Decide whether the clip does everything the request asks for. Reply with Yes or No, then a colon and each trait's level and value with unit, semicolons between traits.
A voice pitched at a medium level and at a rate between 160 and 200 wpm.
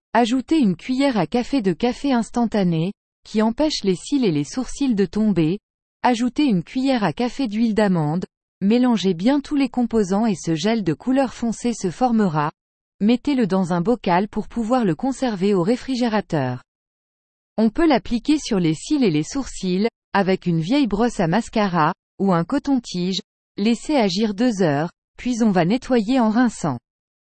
No: high, 220 Hz; average, 165 wpm